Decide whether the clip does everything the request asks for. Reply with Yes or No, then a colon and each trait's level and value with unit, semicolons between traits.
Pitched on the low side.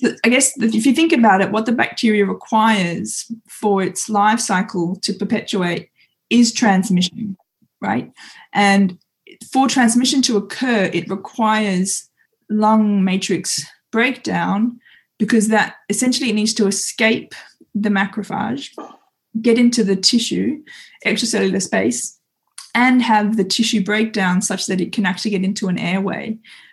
No: high, 215 Hz